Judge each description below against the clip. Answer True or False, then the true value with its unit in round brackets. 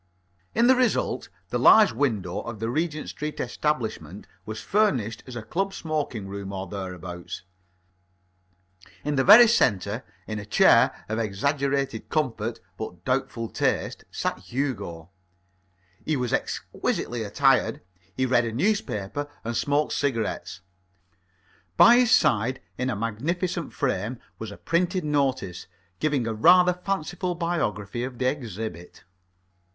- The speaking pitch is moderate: False (125 Hz)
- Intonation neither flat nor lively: False (6.1 semitones)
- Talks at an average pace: False (130 wpm)